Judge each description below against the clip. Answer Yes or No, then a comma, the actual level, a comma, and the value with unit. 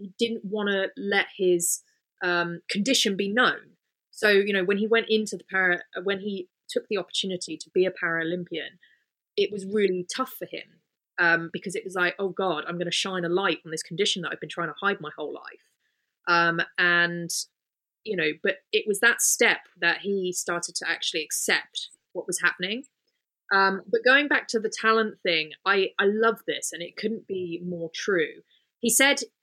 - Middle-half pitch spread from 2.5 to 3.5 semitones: No, average, 3.9 semitones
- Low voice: No, high, 195 Hz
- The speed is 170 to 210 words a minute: Yes, average, 200 wpm